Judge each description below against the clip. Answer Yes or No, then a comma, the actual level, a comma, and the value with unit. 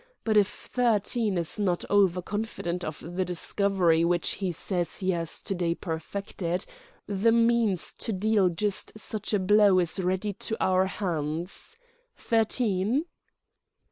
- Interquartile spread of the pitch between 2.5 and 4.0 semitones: Yes, average, 3.2 semitones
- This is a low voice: No, high, 190 Hz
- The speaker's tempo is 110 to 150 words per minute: Yes, average, 140 wpm